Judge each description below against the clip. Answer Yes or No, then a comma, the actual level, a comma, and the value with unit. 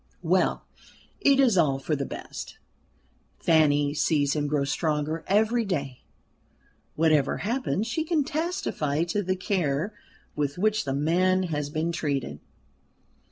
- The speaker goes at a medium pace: No, slow, 130 wpm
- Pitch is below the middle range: No, medium, 160 Hz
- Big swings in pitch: Yes, wide, 5.9 semitones